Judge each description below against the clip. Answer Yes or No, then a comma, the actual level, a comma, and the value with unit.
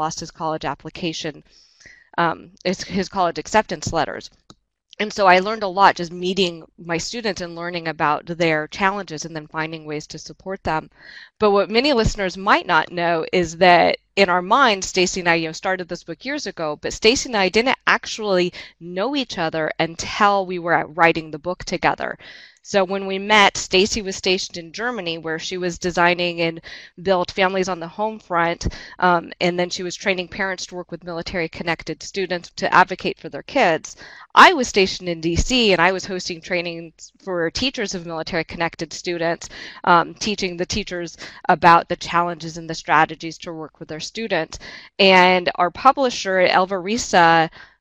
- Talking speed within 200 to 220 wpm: No, average, 180 wpm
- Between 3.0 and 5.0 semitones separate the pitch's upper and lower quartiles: No, narrow, 2.6 semitones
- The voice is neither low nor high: Yes, medium, 180 Hz